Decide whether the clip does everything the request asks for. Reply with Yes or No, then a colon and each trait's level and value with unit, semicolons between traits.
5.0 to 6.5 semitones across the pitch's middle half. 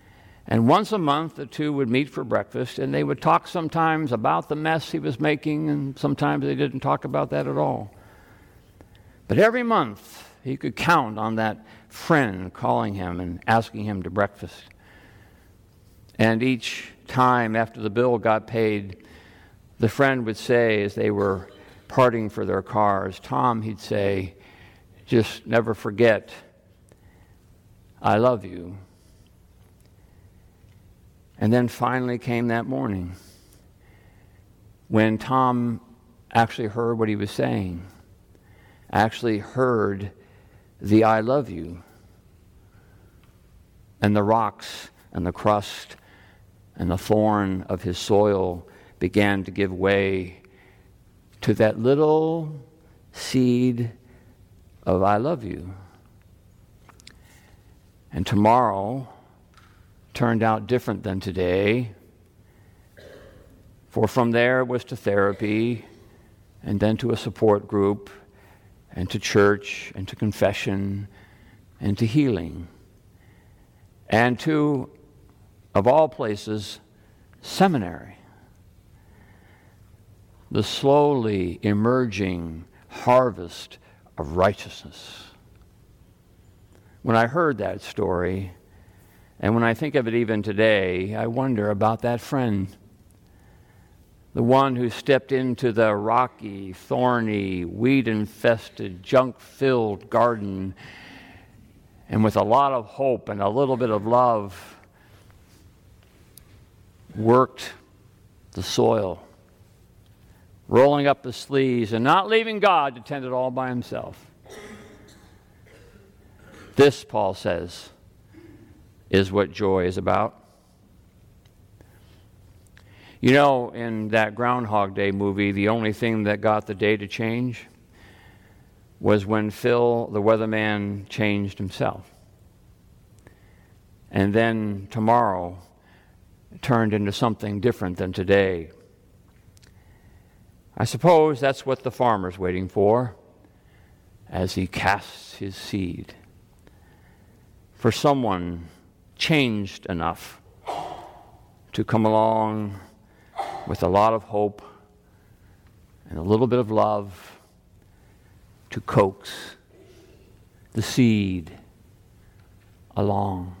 No: average, 3.2 semitones